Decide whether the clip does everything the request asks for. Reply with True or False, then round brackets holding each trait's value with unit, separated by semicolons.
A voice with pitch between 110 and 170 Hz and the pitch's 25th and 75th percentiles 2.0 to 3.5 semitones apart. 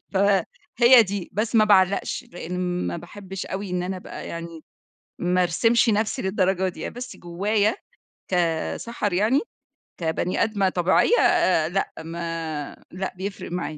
False (190 Hz; 2.8 semitones)